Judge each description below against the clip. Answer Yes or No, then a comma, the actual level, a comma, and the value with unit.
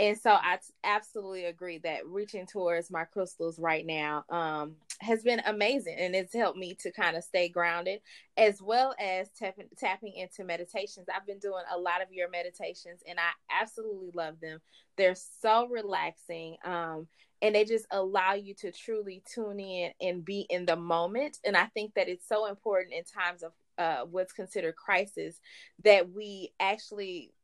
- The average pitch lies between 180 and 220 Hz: Yes, high, 190 Hz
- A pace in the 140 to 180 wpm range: Yes, average, 175 wpm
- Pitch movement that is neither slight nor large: Yes, average, 3.4 semitones